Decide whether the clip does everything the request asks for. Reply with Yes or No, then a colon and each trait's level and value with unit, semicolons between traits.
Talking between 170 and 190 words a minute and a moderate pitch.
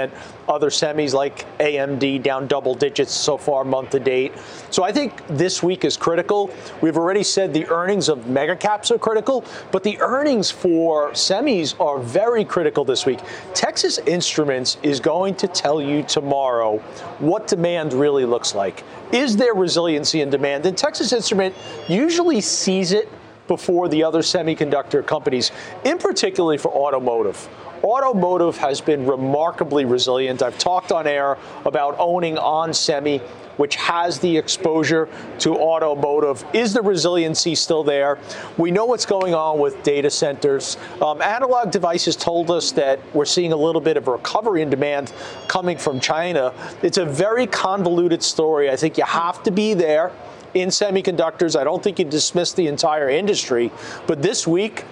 No: average, 160 wpm; medium, 165 Hz